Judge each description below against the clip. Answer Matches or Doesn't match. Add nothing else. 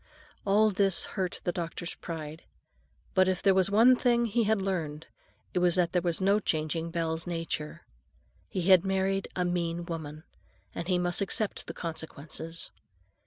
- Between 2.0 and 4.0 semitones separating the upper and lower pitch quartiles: Matches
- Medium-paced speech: Matches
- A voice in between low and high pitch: Matches